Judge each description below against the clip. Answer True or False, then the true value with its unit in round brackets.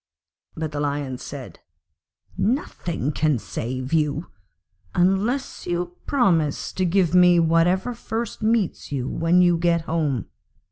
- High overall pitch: False (170 Hz)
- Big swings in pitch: False (3.7 semitones)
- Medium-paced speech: False (125 wpm)